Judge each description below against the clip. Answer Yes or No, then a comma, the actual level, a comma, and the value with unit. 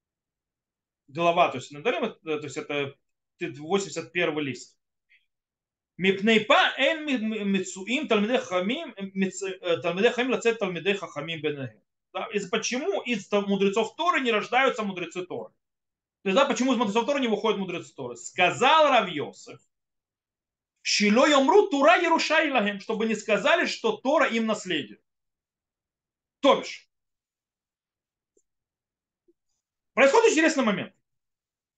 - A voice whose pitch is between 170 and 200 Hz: No, high, 210 Hz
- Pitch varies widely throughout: Yes, wide, 6.5 semitones